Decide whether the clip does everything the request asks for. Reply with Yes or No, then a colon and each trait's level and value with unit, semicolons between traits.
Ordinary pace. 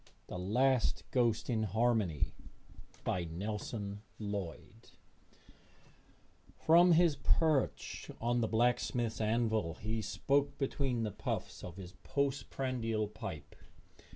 No: slow, 105 wpm